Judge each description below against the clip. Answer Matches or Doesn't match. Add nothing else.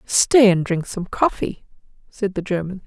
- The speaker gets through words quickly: Doesn't match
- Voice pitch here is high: Matches